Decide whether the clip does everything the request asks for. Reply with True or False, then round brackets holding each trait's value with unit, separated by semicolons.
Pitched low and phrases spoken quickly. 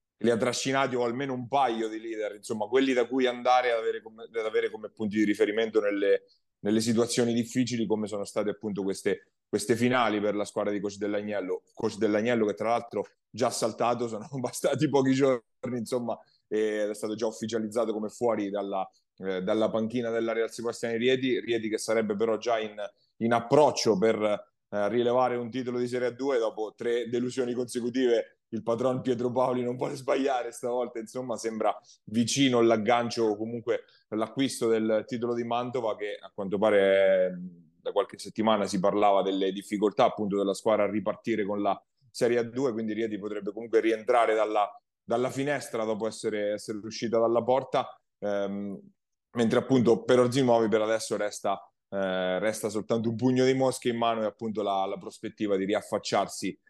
True (115 Hz; 175 wpm)